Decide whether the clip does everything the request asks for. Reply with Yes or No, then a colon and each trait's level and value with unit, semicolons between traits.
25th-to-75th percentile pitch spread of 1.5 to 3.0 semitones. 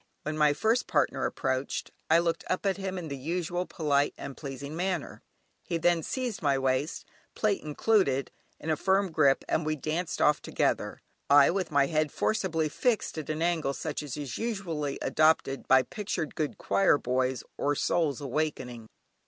No: average, 4.0 semitones